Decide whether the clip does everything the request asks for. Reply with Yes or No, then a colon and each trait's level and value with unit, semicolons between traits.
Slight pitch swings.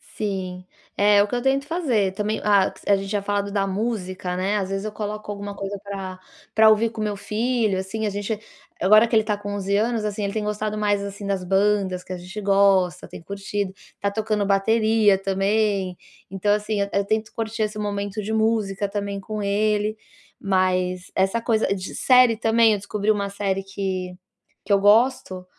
Yes: narrow, 1.7 semitones